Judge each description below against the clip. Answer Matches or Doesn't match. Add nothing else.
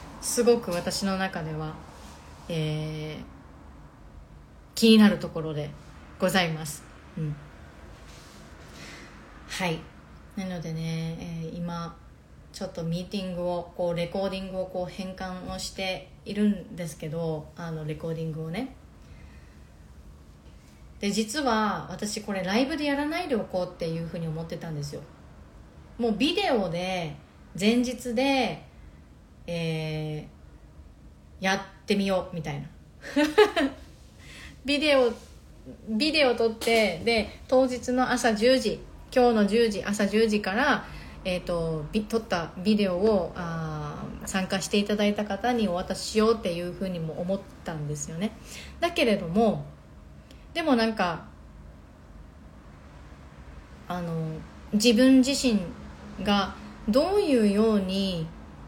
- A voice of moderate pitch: Matches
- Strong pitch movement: Matches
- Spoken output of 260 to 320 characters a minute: Doesn't match